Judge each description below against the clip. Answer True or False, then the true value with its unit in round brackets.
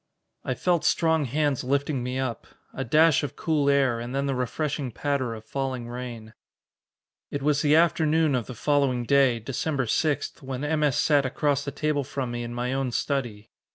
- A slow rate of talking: False (190 wpm)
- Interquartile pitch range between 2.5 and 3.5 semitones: True (2.9 semitones)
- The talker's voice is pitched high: False (135 Hz)